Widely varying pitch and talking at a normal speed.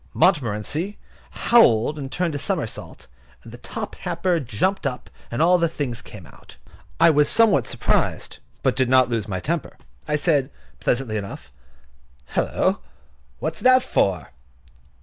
Yes: wide, 7.1 semitones; average, 150 wpm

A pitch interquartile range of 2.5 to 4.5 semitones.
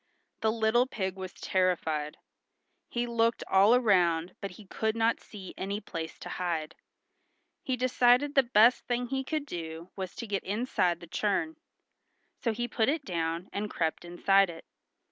No: wide, 5.4 semitones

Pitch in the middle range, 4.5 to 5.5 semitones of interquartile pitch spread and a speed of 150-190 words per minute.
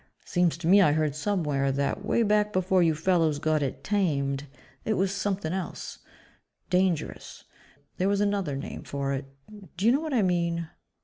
Yes: medium, 175 Hz; average, 5.0 semitones; average, 175 wpm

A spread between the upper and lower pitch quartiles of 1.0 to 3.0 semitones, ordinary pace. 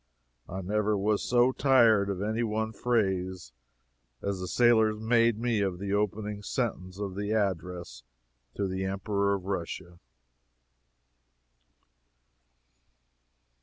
No: narrow, 2.6 semitones; slow, 115 wpm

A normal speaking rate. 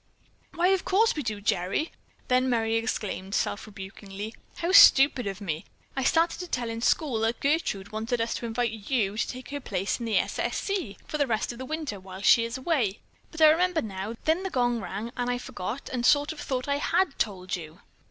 No: fast, 215 wpm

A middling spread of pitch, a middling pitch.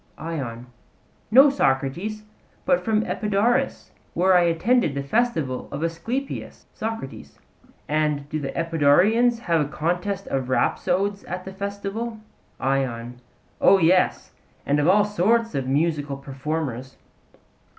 No: wide, 6.9 semitones; medium, 170 Hz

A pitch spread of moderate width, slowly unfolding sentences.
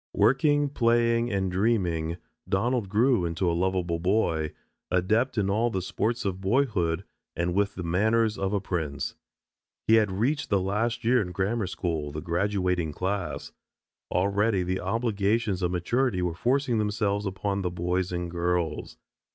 No: average, 4.2 semitones; average, 155 wpm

